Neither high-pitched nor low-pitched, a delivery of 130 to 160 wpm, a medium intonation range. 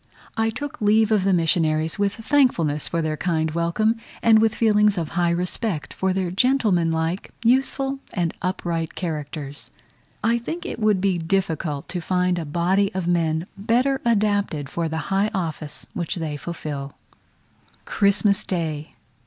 Yes: medium, 180 Hz; average, 150 wpm; average, 4.7 semitones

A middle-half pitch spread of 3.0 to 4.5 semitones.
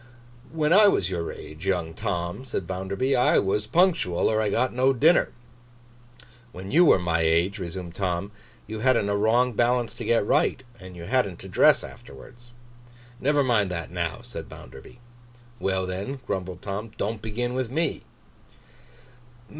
No: wide, 5.4 semitones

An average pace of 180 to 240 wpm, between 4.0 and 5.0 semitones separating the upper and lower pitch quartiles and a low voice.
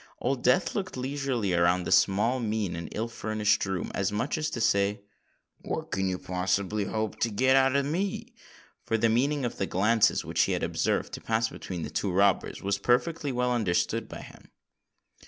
Yes: average, 185 wpm; average, 4.6 semitones; low, 110 Hz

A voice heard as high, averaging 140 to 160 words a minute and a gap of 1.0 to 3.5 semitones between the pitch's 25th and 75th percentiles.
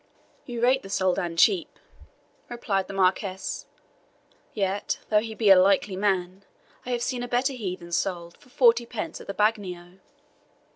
No: high, 200 Hz; average, 155 wpm; average, 4.2 semitones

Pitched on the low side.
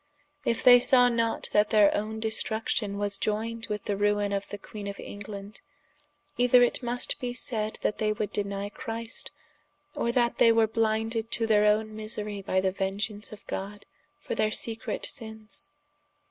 No: high, 215 Hz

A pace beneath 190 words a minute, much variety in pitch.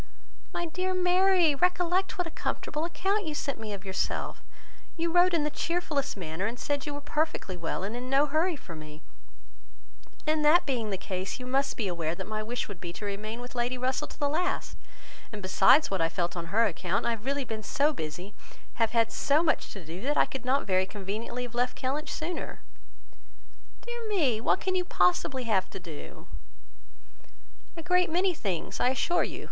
No: average, 200 wpm; wide, 8.3 semitones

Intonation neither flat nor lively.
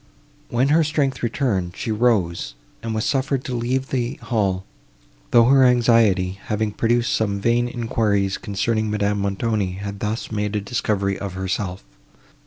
Yes: average, 3.3 semitones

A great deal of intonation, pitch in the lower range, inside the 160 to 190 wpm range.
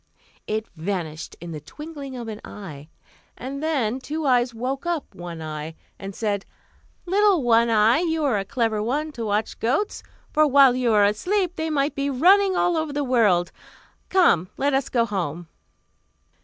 No: wide, 6.7 semitones; high, 245 Hz; average, 170 wpm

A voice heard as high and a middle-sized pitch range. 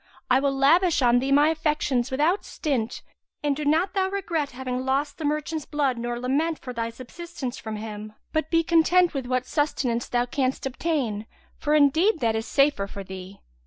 Yes: very high, 275 Hz; average, 4.4 semitones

